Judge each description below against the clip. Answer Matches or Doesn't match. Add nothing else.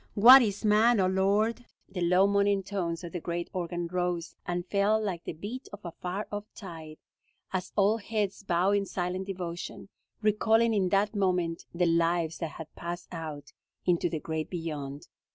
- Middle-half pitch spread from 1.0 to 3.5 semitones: Matches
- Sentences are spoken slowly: Doesn't match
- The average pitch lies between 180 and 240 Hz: Matches